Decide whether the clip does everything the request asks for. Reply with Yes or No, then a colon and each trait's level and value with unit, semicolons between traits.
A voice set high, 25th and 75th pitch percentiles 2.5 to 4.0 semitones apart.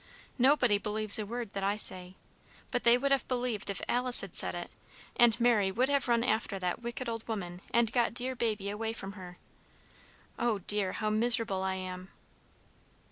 Yes: high, 220 Hz; average, 3.5 semitones